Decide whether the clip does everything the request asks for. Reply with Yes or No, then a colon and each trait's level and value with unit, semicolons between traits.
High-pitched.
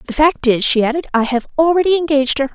Yes: very high, 285 Hz